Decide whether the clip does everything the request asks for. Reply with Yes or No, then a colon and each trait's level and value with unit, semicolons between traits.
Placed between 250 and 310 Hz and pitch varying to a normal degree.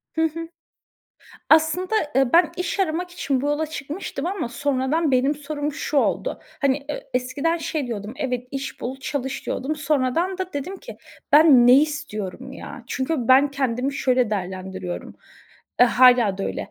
Yes: very high, 280 Hz; average, 3.8 semitones